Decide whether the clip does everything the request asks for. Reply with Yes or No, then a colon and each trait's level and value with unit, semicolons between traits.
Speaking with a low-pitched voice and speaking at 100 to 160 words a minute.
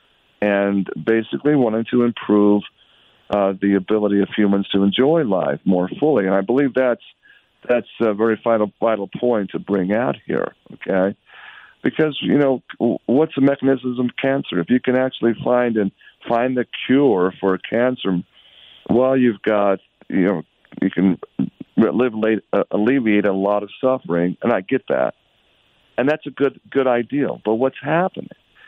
Yes: low, 115 Hz; average, 155 wpm